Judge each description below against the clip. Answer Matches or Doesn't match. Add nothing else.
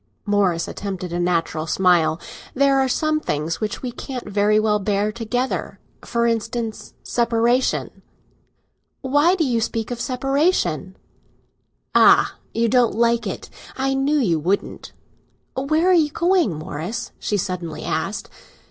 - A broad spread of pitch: Matches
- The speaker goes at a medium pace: Doesn't match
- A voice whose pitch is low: Doesn't match